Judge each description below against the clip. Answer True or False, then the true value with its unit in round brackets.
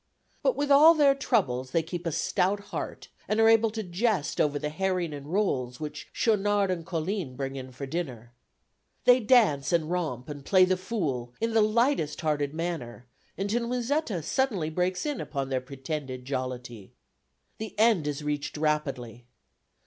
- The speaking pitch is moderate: True (165 Hz)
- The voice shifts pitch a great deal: True (7.5 semitones)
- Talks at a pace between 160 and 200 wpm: True (165 wpm)